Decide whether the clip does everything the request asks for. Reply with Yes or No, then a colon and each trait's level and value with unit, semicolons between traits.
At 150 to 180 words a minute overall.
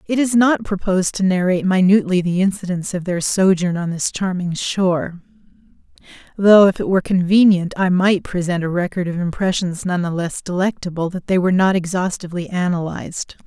Yes: average, 160 wpm